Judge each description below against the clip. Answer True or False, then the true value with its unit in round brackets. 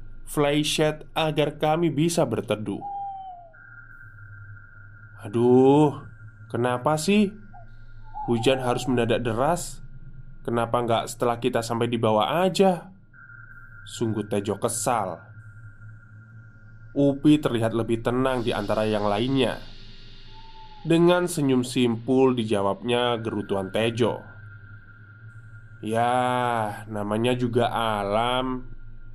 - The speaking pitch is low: True (120 Hz)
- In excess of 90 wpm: False (85 wpm)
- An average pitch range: True (3.3 semitones)